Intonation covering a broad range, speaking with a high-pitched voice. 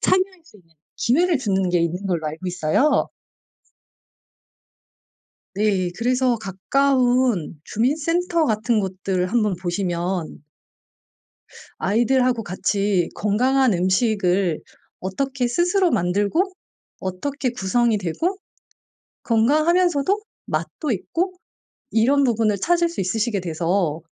Yes: wide, 6.7 semitones; high, 220 Hz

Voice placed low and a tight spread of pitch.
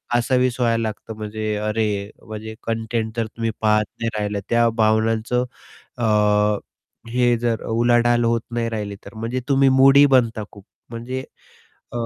Yes: low, 115 Hz; narrow, 1.7 semitones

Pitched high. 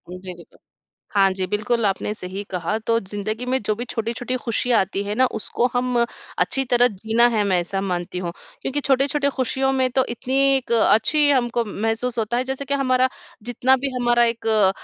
Yes: high, 235 Hz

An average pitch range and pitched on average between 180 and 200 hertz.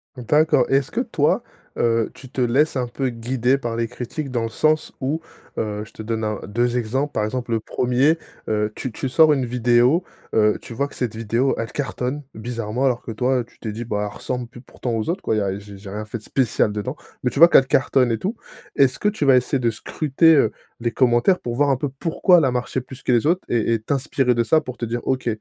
No: average, 3.0 semitones; low, 125 Hz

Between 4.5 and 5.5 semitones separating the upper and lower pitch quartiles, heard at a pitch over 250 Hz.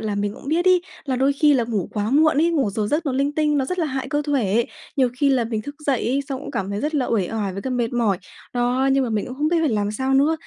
Yes: average, 4.8 semitones; very high, 260 Hz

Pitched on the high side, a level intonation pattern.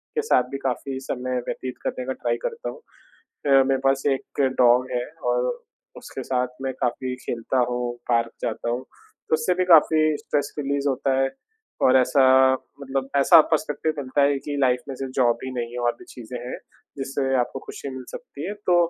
No: low, 135 Hz; narrow, 2.3 semitones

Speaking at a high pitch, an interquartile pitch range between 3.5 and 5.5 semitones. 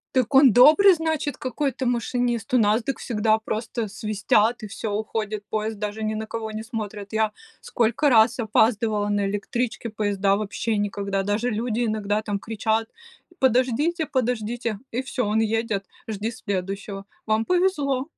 No: high, 220 Hz; average, 2.8 semitones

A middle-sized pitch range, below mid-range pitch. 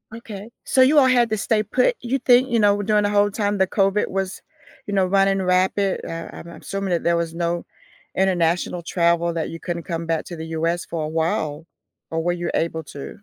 No: average, 3.5 semitones; medium, 185 Hz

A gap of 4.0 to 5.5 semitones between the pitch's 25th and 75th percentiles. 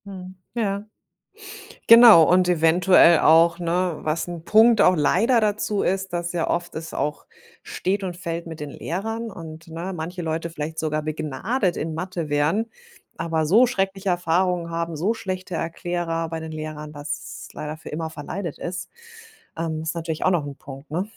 No: average, 2.8 semitones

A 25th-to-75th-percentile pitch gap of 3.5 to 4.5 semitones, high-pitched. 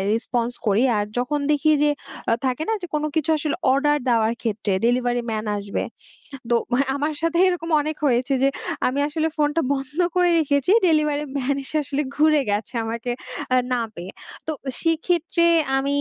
Yes: average, 4.1 semitones; very high, 280 Hz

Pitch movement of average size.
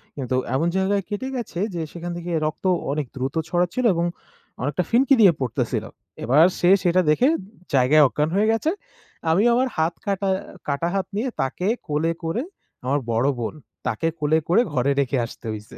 No: wide, 5.8 semitones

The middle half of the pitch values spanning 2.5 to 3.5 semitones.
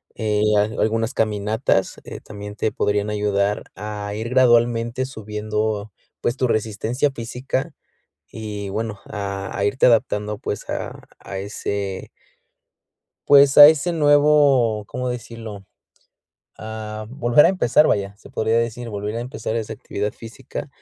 Yes: average, 2.9 semitones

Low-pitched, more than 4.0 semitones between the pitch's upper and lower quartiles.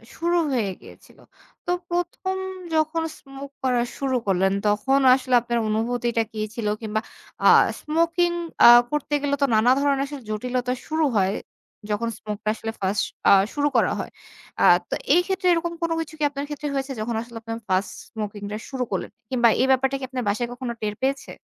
No: very high, 255 Hz; average, 4.7 semitones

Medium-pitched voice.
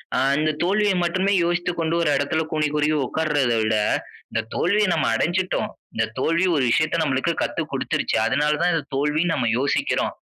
Yes: medium, 160 Hz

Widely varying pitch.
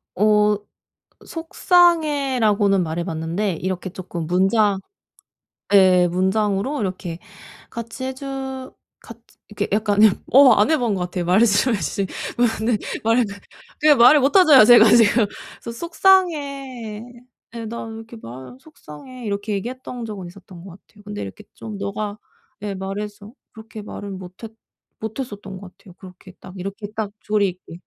No: average, 4.1 semitones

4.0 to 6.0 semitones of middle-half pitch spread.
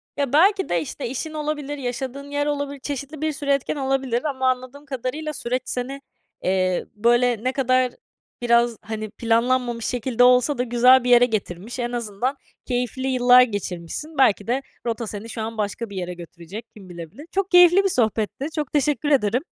No: average, 3.6 semitones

